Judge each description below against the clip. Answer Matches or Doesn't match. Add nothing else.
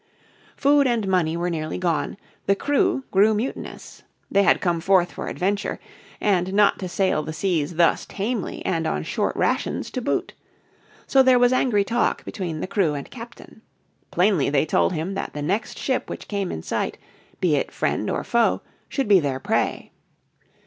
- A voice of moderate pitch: Doesn't match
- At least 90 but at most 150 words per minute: Doesn't match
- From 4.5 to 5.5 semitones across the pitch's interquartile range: Matches